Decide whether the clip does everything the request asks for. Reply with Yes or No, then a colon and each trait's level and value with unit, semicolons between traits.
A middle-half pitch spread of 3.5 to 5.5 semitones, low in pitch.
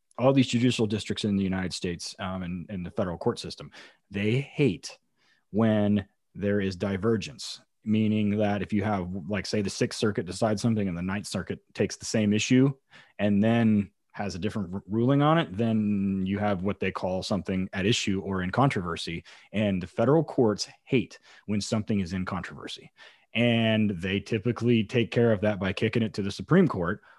No: average, 2.8 semitones; low, 105 Hz